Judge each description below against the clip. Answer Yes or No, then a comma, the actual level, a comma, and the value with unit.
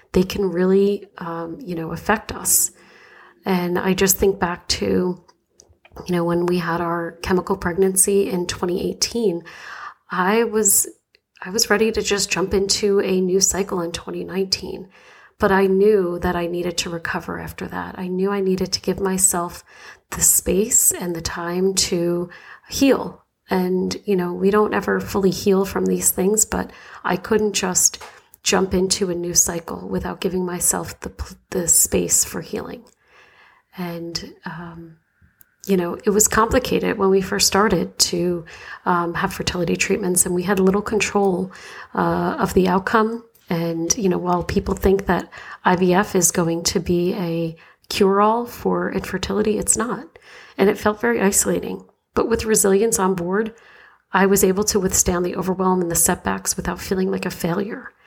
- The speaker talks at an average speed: Yes, average, 165 wpm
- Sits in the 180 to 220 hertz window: Yes, high, 190 Hz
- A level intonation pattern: Yes, narrow, 2.3 semitones